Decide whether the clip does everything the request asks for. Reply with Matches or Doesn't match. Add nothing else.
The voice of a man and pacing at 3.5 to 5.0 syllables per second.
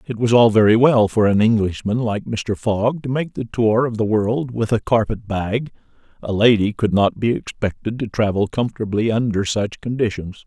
Matches